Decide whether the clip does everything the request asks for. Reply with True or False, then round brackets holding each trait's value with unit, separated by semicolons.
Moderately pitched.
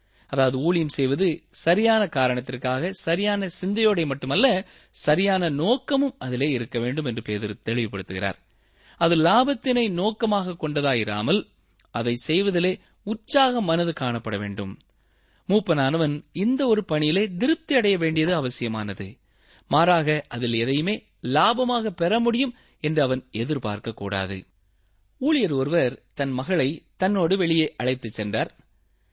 True (155 Hz)